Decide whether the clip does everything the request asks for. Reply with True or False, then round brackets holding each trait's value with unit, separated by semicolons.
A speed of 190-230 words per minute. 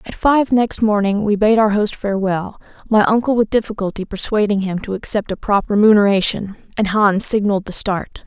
False (180 wpm)